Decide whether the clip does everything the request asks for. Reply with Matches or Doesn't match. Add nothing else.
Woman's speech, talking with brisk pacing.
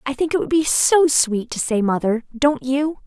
Matches